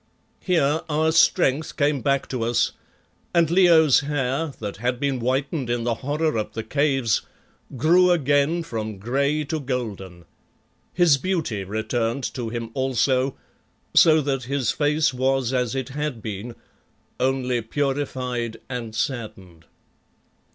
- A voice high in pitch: No, low, 135 Hz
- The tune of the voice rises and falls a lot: No, average, 4.0 semitones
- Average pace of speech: No, slow, 130 wpm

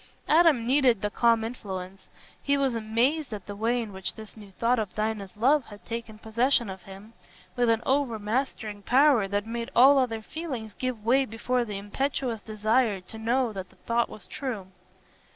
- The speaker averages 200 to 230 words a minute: No, average, 180 wpm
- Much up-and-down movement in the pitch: No, average, 3.3 semitones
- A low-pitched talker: No, high, 230 Hz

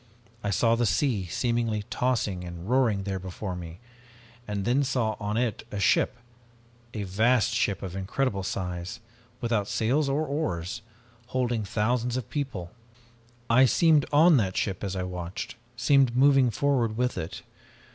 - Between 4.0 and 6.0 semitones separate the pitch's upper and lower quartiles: Yes, average, 4.7 semitones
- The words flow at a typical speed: Yes, average, 150 wpm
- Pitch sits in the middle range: No, low, 115 Hz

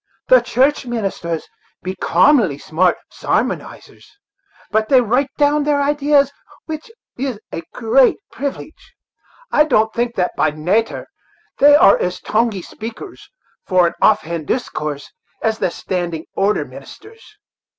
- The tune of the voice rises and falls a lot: Yes, wide, 7.5 semitones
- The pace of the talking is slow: Yes, slow, 130 wpm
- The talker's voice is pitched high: Yes, high, 225 Hz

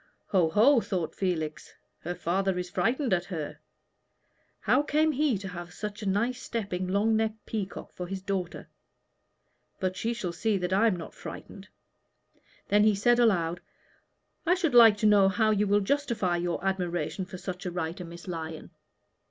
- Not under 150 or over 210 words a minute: Yes, average, 170 wpm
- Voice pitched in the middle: No, high, 195 Hz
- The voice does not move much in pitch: No, average, 3.8 semitones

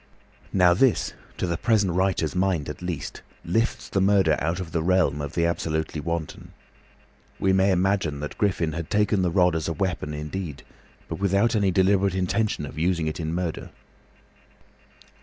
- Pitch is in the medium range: No, very low, 90 Hz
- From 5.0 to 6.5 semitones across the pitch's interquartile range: No, average, 3.2 semitones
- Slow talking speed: No, average, 170 wpm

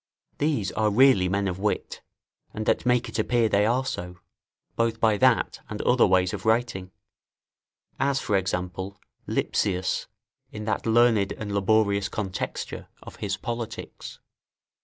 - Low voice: Yes, low, 105 Hz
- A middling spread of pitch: Yes, average, 3.3 semitones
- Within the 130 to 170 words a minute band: Yes, average, 140 wpm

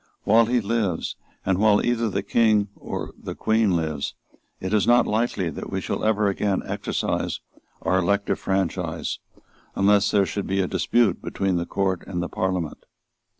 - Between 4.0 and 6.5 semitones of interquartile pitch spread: No, average, 2.8 semitones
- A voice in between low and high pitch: No, low, 100 Hz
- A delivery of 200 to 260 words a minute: No, average, 165 wpm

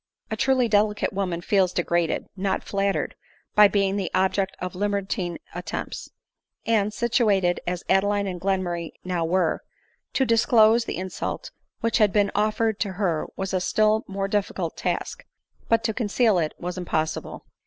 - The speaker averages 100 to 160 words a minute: Yes, average, 155 wpm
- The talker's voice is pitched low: No, high, 195 Hz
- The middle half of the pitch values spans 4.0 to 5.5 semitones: No, average, 2.8 semitones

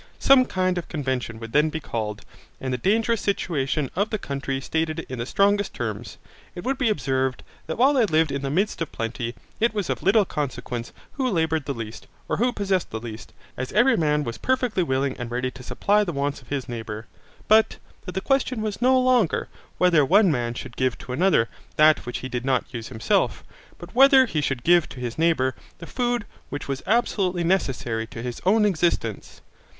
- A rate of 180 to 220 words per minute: Yes, fast, 205 wpm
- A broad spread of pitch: Yes, wide, 8.2 semitones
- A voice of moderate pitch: Yes, medium, 155 Hz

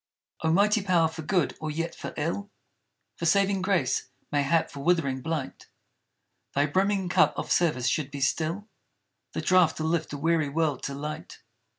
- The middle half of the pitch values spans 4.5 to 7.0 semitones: No, average, 3.7 semitones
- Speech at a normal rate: Yes, average, 170 wpm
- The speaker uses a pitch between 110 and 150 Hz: No, medium, 160 Hz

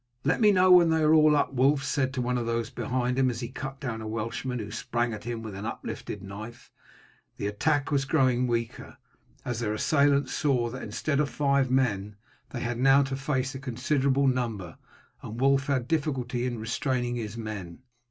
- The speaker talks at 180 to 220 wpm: Yes, average, 195 wpm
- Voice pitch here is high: No, low, 125 Hz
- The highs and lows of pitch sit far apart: No, average, 3.1 semitones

